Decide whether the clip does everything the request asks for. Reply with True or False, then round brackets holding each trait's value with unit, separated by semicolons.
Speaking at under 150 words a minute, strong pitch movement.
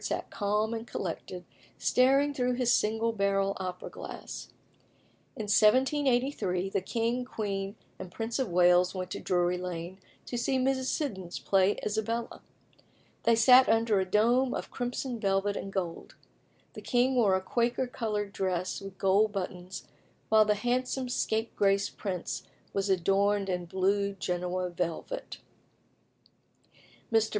False (135 wpm; 4.1 semitones)